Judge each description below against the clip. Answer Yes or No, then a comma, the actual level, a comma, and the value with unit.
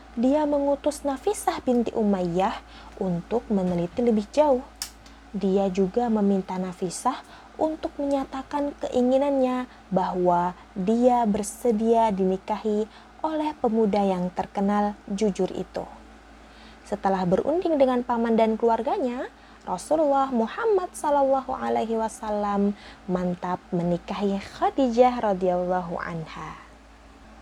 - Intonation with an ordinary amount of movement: No, wide, 5.7 semitones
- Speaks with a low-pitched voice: No, high, 225 Hz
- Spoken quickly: No, average, 90 wpm